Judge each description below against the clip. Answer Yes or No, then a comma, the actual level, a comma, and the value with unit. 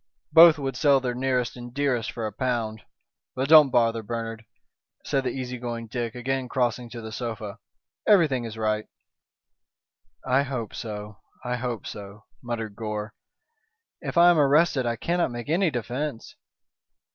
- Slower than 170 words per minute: Yes, average, 155 wpm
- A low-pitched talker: Yes, low, 120 Hz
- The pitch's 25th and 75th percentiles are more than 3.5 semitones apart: No, average, 3.0 semitones